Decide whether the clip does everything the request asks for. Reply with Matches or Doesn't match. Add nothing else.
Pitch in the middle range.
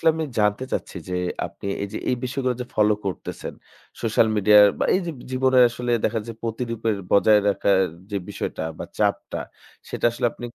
Doesn't match